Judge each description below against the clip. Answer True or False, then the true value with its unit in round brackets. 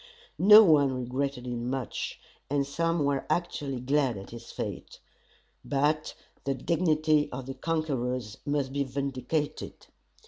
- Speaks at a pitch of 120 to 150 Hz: True (140 Hz)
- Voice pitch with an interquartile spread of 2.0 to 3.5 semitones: True (2.8 semitones)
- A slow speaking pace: True (130 wpm)